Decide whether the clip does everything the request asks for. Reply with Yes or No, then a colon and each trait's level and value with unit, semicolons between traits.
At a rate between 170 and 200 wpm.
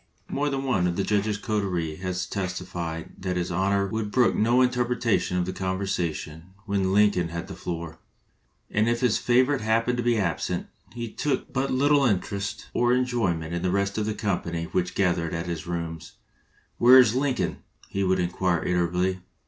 Yes: average, 175 wpm